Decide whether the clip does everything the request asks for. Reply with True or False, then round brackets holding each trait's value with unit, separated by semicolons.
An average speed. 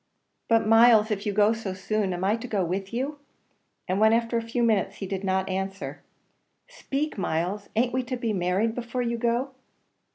True (195 wpm)